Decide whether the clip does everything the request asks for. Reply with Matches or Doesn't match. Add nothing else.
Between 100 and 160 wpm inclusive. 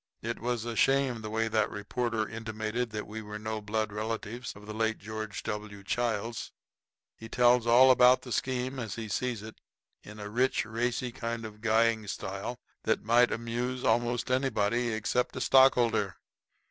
Doesn't match